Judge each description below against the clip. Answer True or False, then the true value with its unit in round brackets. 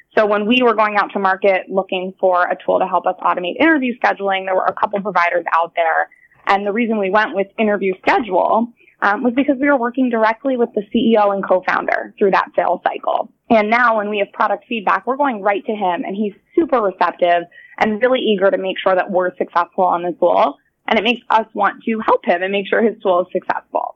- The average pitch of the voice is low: False (205 Hz)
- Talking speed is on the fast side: True (230 wpm)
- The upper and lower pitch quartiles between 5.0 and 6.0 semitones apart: False (4.2 semitones)